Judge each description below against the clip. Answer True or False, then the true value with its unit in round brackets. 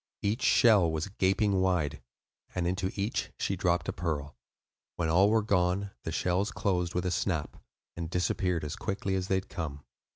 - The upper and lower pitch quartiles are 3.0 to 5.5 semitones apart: False (2.5 semitones)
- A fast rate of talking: False (175 wpm)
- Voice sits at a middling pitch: False (90 Hz)